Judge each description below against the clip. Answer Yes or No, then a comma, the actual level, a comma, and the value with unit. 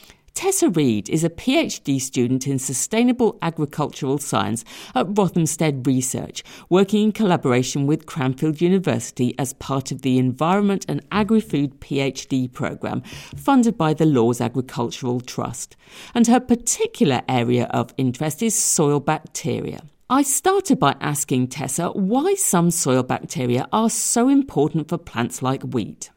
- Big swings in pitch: Yes, wide, 8.0 semitones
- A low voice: No, medium, 150 Hz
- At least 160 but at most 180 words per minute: No, slow, 135 wpm